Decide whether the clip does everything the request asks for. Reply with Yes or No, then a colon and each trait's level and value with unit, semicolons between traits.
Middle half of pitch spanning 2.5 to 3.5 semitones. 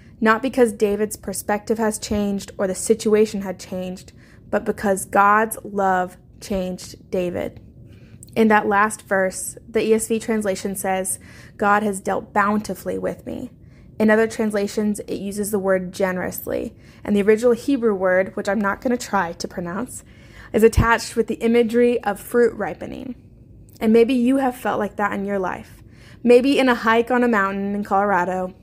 Yes: average, 2.9 semitones